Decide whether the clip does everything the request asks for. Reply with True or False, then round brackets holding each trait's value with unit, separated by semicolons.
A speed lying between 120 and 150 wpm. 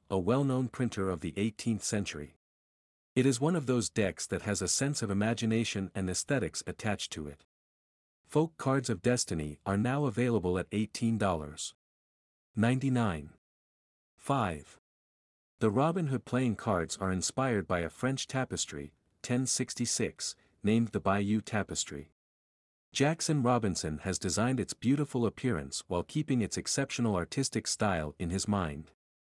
True (135 wpm)